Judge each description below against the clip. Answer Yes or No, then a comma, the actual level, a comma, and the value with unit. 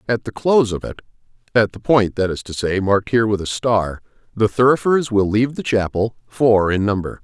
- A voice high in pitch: No, low, 110 Hz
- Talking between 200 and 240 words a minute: Yes, fast, 205 wpm